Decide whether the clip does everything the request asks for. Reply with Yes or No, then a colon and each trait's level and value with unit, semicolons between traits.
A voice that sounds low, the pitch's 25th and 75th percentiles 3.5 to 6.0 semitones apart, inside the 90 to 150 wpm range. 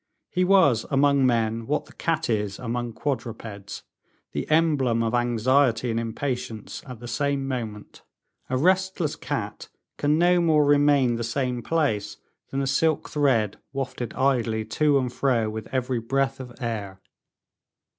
Yes: low, 130 Hz; average, 3.9 semitones; average, 145 wpm